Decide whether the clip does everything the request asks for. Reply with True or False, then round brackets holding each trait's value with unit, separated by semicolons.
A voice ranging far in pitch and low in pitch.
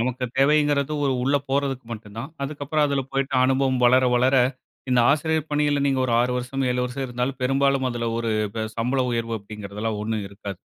False (3.0 semitones; 130 Hz)